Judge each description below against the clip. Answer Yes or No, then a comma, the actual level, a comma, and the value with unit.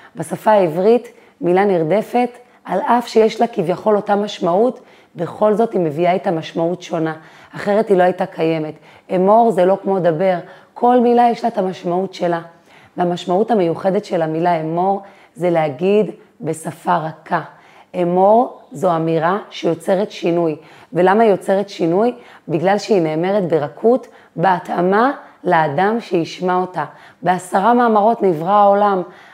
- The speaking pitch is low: No, medium, 185 Hz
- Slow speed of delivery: No, average, 135 wpm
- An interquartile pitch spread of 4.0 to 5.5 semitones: No, average, 3.6 semitones